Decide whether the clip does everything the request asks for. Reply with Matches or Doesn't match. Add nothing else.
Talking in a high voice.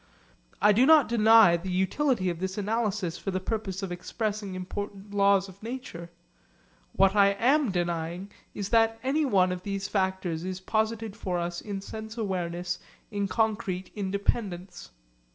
Matches